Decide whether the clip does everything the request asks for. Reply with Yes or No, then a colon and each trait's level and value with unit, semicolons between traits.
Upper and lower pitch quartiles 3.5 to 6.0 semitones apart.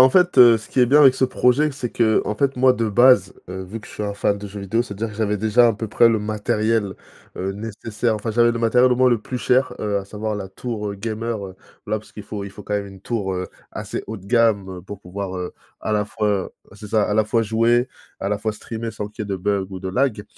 No: narrow, 2.6 semitones